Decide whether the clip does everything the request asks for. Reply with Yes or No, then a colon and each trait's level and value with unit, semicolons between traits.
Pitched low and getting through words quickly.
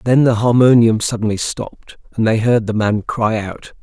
No: low, 110 Hz; average, 190 wpm